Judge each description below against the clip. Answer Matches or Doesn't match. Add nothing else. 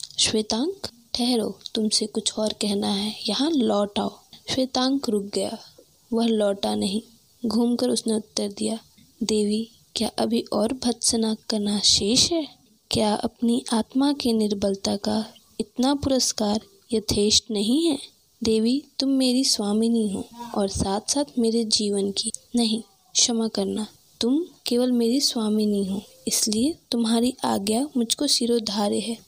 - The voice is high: Matches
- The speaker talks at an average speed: Matches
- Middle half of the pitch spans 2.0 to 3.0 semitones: Matches